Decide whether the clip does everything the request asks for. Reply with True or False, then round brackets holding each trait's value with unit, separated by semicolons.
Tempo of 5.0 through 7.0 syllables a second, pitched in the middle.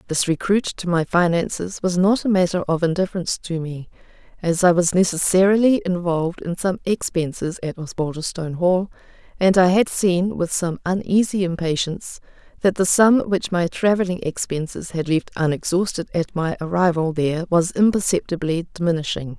True (5.2 syllables/s; 180 Hz)